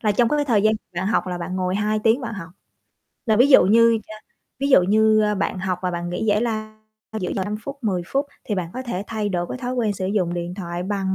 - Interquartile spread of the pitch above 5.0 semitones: No, average, 3.7 semitones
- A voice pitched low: No, high, 210 Hz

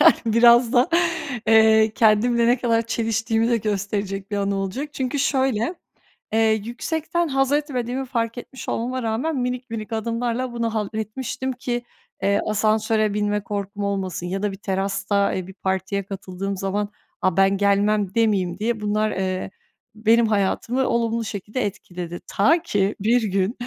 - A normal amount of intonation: Yes, average, 3.2 semitones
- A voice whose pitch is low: No, high, 220 Hz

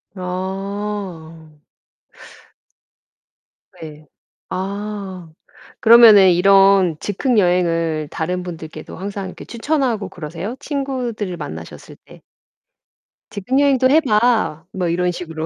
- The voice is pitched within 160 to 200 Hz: Yes, high, 190 Hz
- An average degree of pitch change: Yes, average, 3.8 semitones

